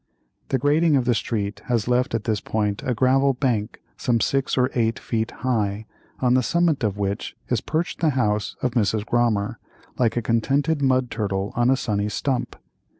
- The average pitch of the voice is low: Yes, low, 120 Hz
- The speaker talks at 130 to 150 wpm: No, average, 185 wpm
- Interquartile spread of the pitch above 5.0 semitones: No, average, 3.5 semitones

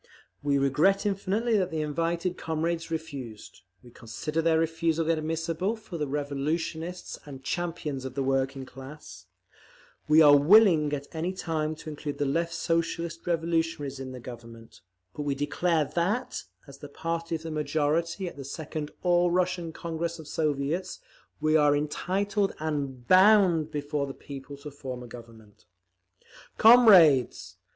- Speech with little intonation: No, average, 3.2 semitones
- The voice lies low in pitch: No, medium, 155 Hz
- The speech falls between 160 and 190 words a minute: No, average, 145 wpm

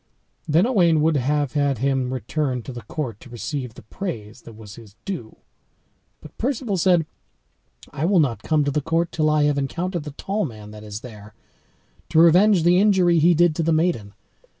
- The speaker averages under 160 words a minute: No, average, 195 wpm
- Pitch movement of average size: No, wide, 6.0 semitones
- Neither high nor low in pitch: Yes, medium, 150 Hz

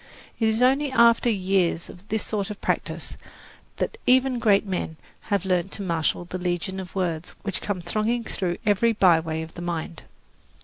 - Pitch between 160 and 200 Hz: Yes, high, 190 Hz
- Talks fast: No, average, 175 wpm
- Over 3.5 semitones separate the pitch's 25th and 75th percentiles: Yes, average, 4.0 semitones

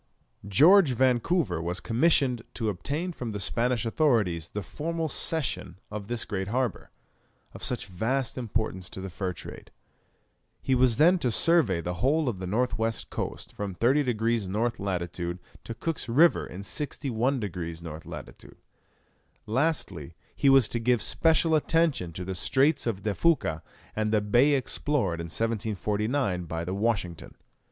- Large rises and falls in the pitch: Yes, wide, 6.3 semitones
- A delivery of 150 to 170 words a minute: Yes, average, 155 wpm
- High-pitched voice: No, low, 115 Hz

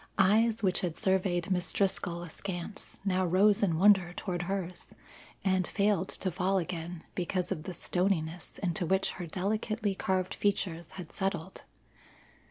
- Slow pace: No, average, 145 wpm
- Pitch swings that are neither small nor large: No, narrow, 2.0 semitones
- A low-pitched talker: No, medium, 185 Hz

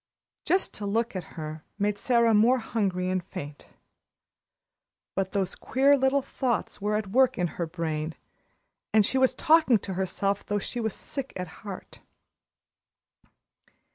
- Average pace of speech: Yes, average, 145 wpm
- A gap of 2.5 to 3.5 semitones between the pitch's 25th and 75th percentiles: No, average, 5.1 semitones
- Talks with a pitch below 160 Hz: No, high, 205 Hz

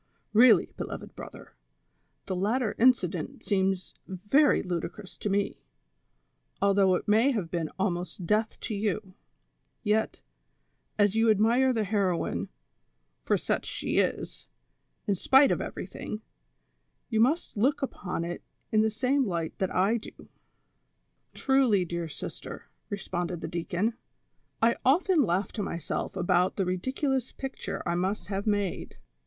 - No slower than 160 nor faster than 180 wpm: No, slow, 135 wpm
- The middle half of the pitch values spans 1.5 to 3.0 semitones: No, average, 4.0 semitones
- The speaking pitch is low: No, high, 205 Hz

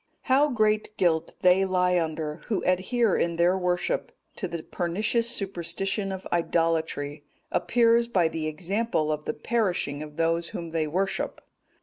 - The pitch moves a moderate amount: Yes, average, 4.1 semitones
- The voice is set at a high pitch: No, medium, 180 Hz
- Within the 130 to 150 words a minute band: Yes, average, 145 wpm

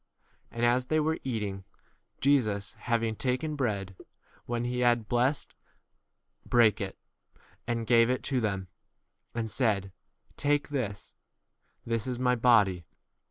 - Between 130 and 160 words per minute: Yes, slow, 135 wpm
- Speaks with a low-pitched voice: Yes, low, 120 Hz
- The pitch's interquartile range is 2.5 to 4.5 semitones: Yes, average, 3.1 semitones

